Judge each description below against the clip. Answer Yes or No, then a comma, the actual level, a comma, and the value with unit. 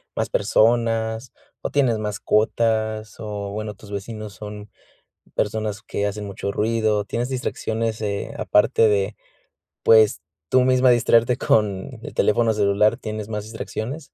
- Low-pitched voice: Yes, low, 110 Hz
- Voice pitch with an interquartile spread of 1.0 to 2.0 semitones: Yes, narrow, 1.7 semitones